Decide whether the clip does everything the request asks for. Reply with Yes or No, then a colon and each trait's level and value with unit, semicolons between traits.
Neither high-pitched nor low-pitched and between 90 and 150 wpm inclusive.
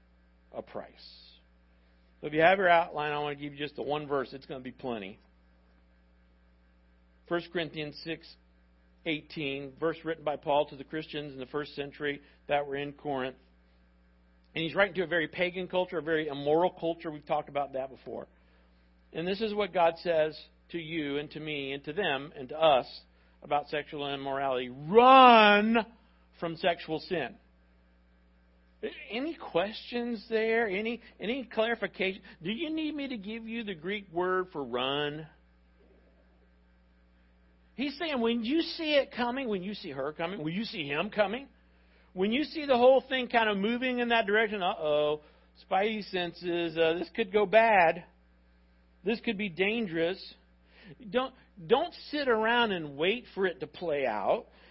No: medium, 155 Hz; average, 165 wpm